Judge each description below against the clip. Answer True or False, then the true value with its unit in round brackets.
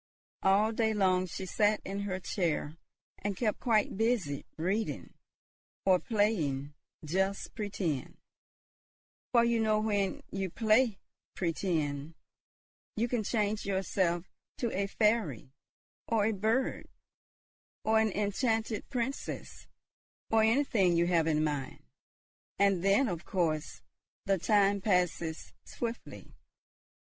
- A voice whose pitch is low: False (200 Hz)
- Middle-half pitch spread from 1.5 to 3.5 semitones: False (4.0 semitones)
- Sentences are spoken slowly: True (115 wpm)